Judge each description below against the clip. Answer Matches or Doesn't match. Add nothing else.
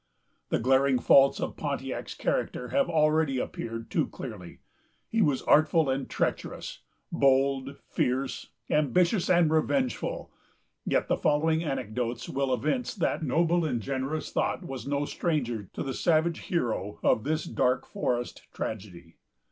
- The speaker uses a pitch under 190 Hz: Matches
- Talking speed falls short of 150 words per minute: Matches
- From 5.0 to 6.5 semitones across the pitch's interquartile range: Doesn't match